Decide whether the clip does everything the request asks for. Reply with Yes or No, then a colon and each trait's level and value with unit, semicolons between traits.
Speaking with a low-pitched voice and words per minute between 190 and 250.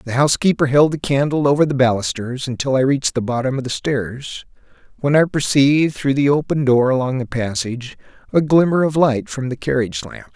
Yes: low, 130 Hz; average, 195 wpm